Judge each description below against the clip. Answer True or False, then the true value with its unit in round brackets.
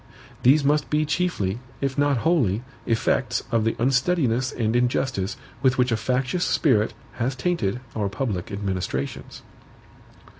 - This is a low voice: True (125 Hz)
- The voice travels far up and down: False (4.4 semitones)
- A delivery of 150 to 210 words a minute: False (135 wpm)